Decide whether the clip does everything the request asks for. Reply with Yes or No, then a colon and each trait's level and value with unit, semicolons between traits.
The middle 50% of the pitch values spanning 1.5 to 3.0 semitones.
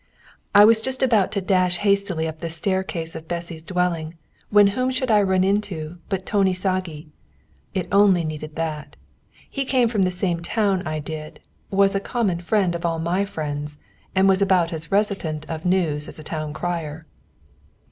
No: average, 3.6 semitones